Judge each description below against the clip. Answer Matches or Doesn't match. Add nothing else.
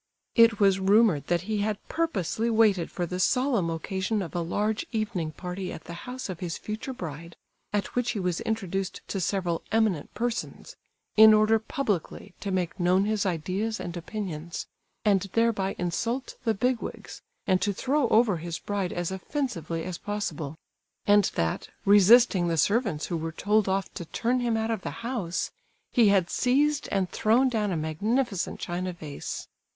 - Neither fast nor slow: Matches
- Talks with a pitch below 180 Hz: Doesn't match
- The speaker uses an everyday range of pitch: Matches